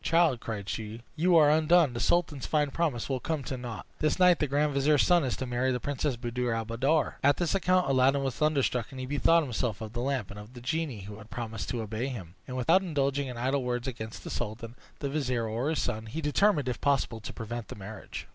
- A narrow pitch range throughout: No, average, 4.4 semitones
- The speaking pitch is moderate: No, low, 130 Hz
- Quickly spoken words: Yes, fast, 240 wpm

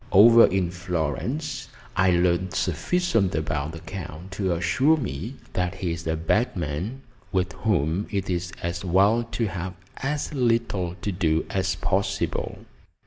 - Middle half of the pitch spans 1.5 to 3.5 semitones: No, average, 4.2 semitones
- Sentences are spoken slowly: No, average, 145 wpm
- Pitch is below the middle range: Yes, very low, 95 Hz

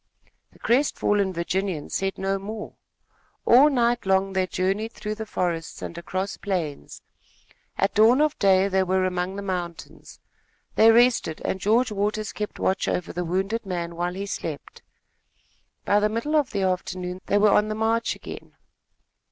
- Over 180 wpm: No, average, 160 wpm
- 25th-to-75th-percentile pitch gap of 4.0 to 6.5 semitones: No, average, 2.9 semitones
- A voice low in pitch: No, high, 195 Hz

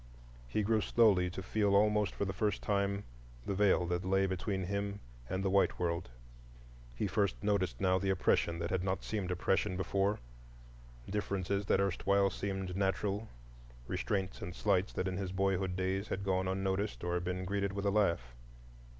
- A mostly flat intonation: Yes, narrow, 1.4 semitones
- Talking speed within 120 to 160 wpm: No, average, 170 wpm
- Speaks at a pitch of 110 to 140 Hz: No, very low, 95 Hz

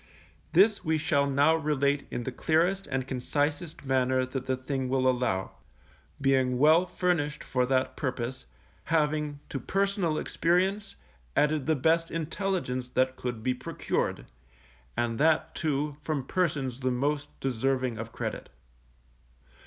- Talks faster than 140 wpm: No, slow, 135 wpm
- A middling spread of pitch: Yes, average, 3.8 semitones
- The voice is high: No, medium, 140 Hz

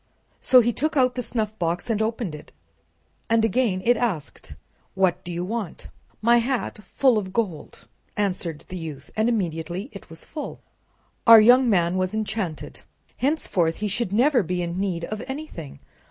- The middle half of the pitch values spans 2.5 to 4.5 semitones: No, average, 5.2 semitones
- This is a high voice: Yes, high, 210 Hz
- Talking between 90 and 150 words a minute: No, average, 165 wpm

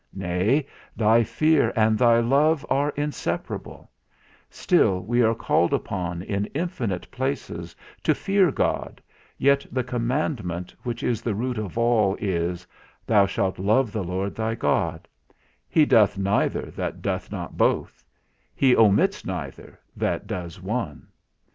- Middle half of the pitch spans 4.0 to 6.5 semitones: Yes, wide, 5.4 semitones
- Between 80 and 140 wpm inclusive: Yes, slow, 135 wpm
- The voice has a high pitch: No, low, 110 Hz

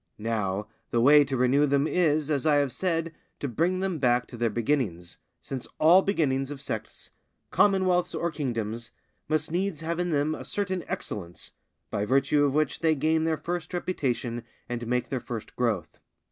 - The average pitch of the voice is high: No, medium, 145 Hz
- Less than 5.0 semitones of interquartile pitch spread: No, average, 5.3 semitones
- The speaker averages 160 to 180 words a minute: Yes, average, 175 wpm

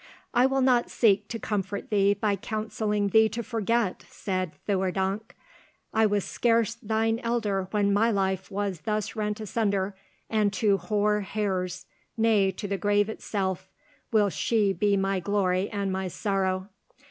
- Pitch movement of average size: No, narrow, 2.2 semitones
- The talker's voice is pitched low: No, high, 205 Hz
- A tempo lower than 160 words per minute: Yes, average, 150 wpm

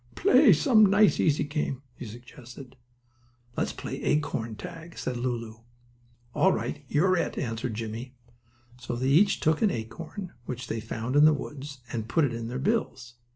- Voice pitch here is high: No, low, 130 Hz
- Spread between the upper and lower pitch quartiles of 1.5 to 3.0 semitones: No, average, 5.0 semitones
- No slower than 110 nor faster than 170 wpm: Yes, average, 165 wpm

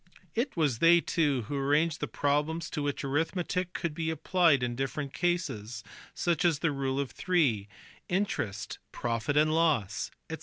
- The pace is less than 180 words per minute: Yes, average, 155 wpm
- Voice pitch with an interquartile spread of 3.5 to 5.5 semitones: Yes, average, 3.9 semitones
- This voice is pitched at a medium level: Yes, medium, 150 Hz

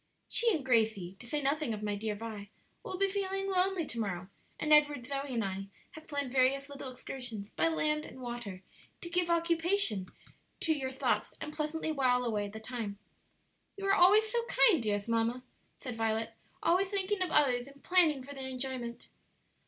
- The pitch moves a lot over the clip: Yes, wide, 6.5 semitones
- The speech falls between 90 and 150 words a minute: No, average, 185 wpm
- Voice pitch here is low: No, very high, 270 Hz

